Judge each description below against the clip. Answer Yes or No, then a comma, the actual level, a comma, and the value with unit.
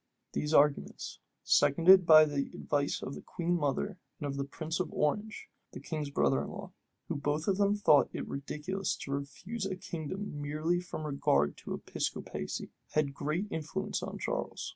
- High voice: No, medium, 155 Hz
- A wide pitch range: No, average, 4.4 semitones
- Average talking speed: Yes, average, 170 wpm